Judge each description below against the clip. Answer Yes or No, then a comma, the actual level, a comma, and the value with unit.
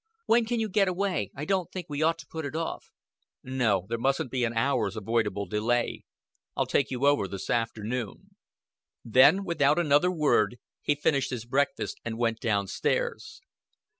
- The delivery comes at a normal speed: Yes, average, 170 wpm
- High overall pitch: No, low, 130 Hz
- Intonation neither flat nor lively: No, wide, 6.3 semitones